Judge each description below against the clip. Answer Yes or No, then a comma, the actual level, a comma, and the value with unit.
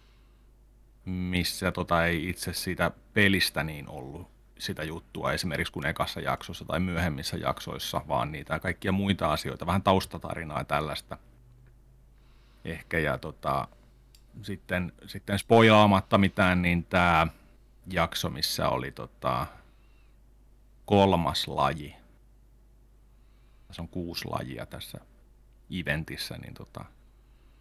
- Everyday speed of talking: Yes, average, 105 wpm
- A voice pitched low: Yes, very low, 90 Hz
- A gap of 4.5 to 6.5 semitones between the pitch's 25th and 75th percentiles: Yes, wide, 5.4 semitones